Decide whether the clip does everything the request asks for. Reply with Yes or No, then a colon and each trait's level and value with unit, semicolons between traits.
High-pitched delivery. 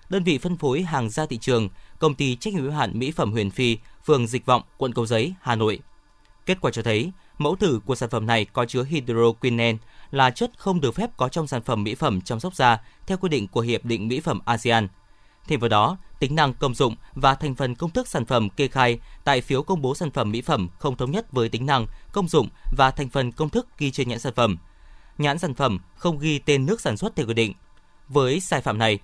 No: low, 130 Hz